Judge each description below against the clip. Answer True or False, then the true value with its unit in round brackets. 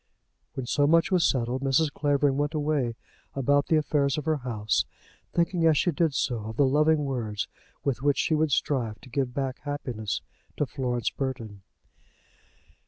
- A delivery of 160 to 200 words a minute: True (170 wpm)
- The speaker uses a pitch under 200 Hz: True (140 Hz)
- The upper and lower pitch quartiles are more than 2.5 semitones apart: True (3.3 semitones)